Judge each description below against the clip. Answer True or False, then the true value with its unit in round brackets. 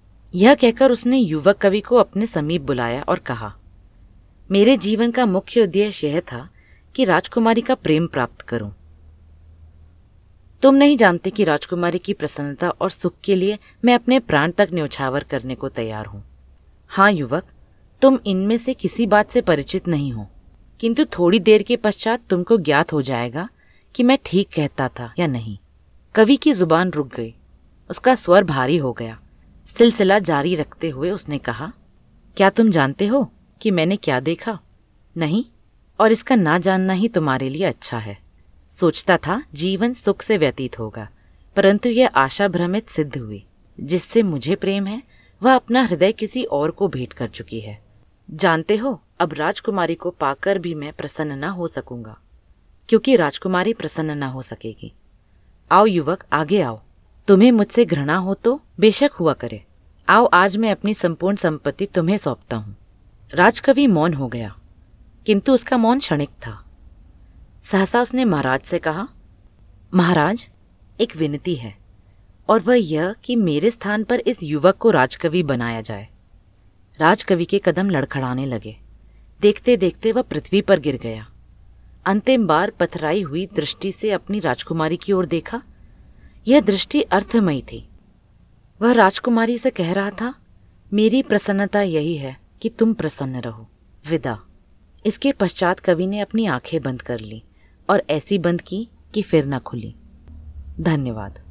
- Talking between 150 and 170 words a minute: True (155 wpm)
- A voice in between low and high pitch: True (170 Hz)